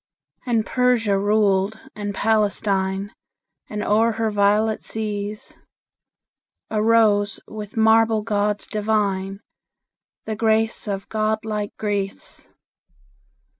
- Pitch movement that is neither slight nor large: No, narrow, 1.4 semitones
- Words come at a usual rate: No, slow, 95 wpm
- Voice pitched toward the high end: Yes, high, 210 Hz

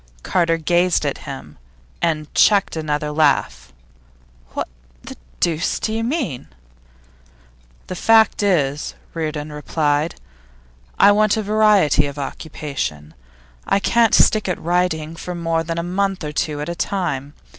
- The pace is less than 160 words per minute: Yes, slow, 135 wpm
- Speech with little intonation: No, average, 4.6 semitones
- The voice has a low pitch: No, medium, 165 Hz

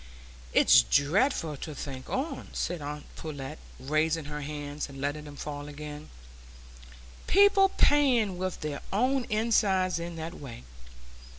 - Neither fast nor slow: No, slow, 130 wpm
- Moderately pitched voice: Yes, medium, 155 Hz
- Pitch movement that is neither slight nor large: No, wide, 5.7 semitones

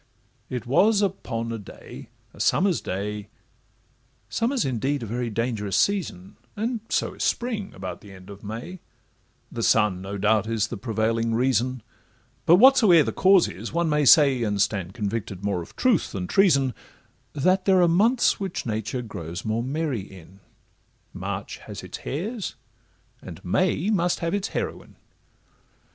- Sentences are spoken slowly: No, average, 155 wpm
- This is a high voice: No, low, 125 Hz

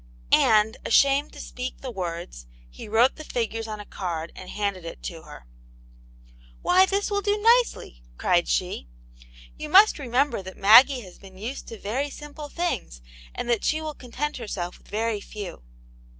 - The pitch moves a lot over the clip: Yes, wide, 7.6 semitones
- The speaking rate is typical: Yes, average, 170 wpm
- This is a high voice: Yes, high, 225 Hz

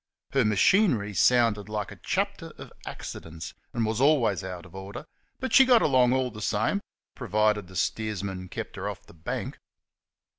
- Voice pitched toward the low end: Yes, low, 105 Hz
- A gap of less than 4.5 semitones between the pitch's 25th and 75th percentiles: No, average, 4.8 semitones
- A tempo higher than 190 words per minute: No, average, 165 wpm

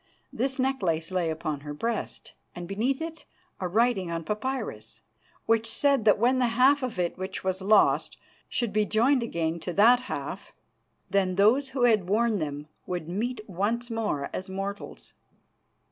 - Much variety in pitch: No, average, 5.0 semitones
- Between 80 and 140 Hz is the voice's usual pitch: No, high, 210 Hz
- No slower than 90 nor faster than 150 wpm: No, average, 160 wpm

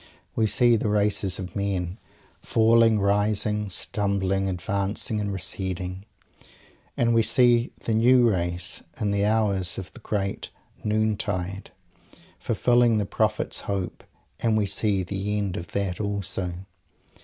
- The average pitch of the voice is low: Yes, low, 100 Hz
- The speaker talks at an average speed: No, slow, 130 wpm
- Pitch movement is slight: Yes, narrow, 2.2 semitones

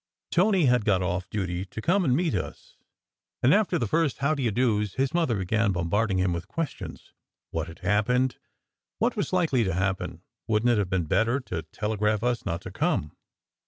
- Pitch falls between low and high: No, low, 110 Hz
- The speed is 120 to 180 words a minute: No, average, 200 wpm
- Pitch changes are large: Yes, wide, 5.7 semitones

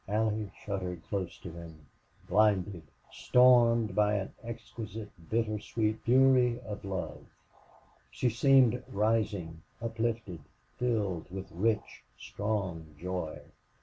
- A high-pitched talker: No, low, 105 Hz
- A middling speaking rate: No, slow, 105 wpm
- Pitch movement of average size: Yes, average, 3.8 semitones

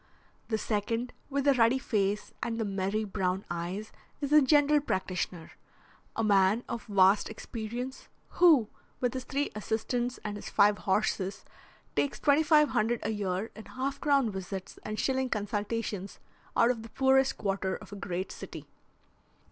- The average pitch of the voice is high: Yes, high, 220 Hz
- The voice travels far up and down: No, average, 4.7 semitones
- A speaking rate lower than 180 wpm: Yes, average, 155 wpm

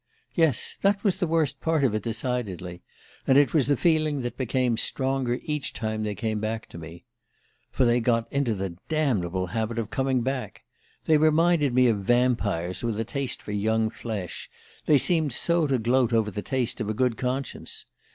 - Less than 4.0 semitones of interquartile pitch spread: No, average, 4.5 semitones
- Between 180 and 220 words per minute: Yes, average, 190 wpm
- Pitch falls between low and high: No, low, 125 Hz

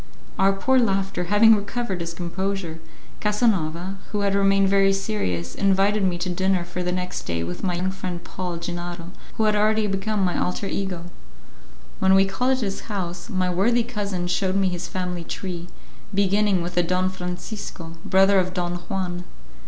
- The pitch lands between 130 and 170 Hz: No, high, 190 Hz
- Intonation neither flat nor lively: No, narrow, 2.1 semitones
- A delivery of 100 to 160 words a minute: No, average, 175 wpm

